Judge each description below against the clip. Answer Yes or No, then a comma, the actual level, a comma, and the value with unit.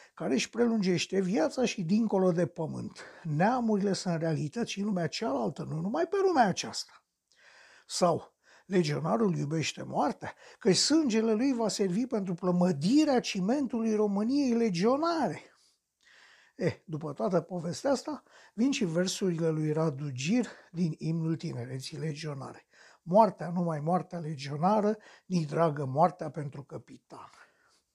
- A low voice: No, medium, 185 Hz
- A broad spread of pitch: Yes, wide, 5.7 semitones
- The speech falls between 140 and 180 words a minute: No, average, 130 wpm